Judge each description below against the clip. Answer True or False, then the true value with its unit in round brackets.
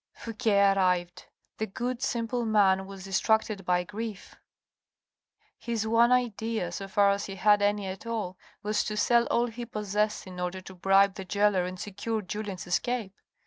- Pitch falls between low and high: False (205 Hz)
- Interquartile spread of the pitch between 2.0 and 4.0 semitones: True (2.8 semitones)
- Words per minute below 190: True (165 wpm)